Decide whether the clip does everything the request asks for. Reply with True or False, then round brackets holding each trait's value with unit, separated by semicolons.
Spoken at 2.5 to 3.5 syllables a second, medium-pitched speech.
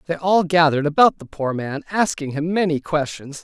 False (5.4 syllables/s; 160 Hz)